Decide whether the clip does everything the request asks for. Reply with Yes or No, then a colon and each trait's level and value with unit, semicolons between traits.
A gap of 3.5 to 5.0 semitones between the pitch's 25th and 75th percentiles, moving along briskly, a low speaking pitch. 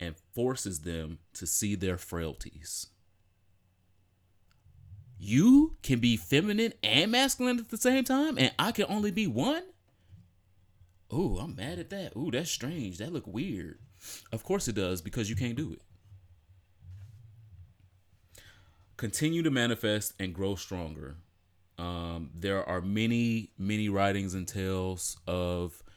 No: average, 4.5 semitones; slow, 135 wpm; low, 100 Hz